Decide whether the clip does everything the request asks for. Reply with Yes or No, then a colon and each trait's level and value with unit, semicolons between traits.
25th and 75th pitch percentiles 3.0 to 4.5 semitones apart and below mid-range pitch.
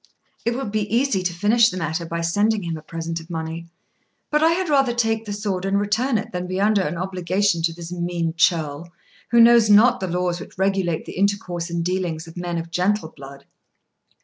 No: average, 4.0 semitones; medium, 185 Hz